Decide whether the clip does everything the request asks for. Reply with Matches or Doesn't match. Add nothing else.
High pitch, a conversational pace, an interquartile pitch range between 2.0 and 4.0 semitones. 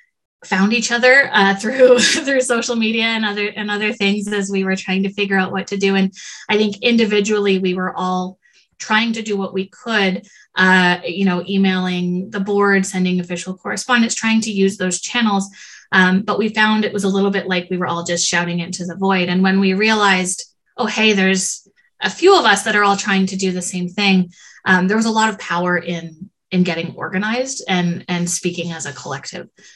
Doesn't match